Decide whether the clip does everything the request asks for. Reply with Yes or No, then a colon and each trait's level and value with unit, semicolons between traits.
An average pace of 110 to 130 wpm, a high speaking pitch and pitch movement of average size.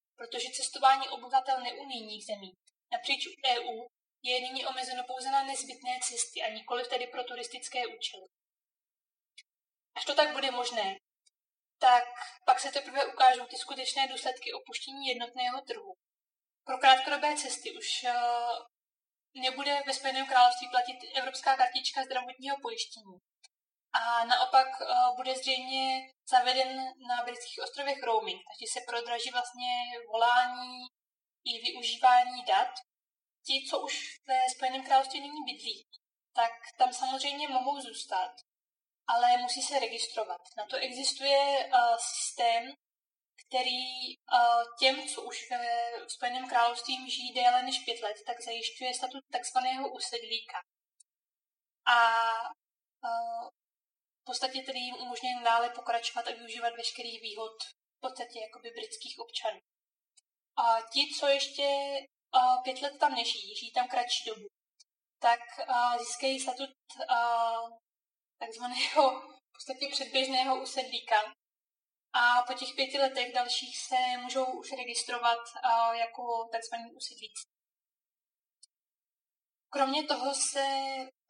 No: average, 120 wpm; very high, 255 Hz; narrow, 2.1 semitones